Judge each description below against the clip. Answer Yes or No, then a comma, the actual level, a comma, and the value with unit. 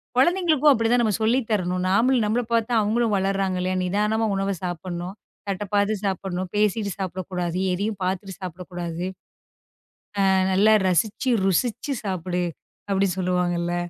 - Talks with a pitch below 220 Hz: Yes, high, 195 Hz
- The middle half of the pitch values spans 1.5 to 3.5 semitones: Yes, average, 3.2 semitones